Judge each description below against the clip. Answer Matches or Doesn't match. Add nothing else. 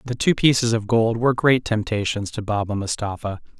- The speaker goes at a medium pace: Matches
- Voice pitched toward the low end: Matches